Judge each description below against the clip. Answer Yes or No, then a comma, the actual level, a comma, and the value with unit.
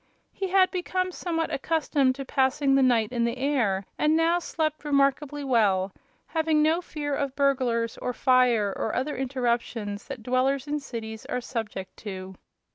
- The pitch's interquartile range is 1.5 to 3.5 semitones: No, average, 4.3 semitones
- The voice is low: No, very high, 265 Hz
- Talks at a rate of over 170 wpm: No, average, 160 wpm